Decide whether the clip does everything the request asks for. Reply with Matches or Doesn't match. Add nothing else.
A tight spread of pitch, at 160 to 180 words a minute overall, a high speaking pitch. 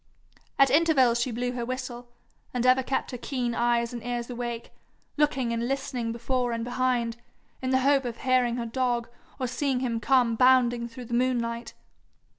Matches